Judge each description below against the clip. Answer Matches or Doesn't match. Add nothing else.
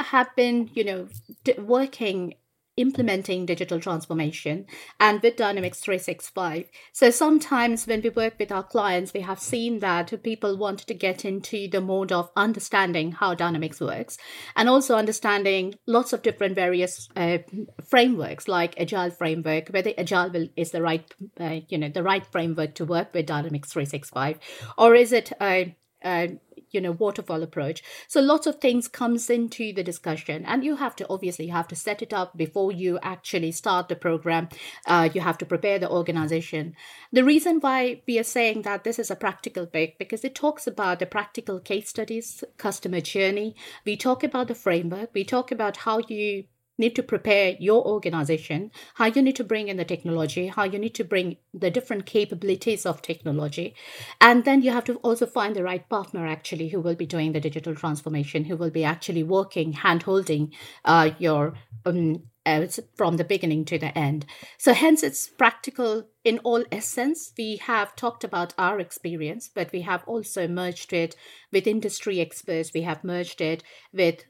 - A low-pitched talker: Doesn't match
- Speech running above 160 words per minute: Matches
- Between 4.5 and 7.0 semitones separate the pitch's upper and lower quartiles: Matches